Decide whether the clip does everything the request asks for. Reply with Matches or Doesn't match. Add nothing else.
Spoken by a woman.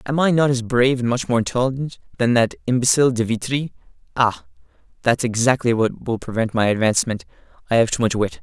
Doesn't match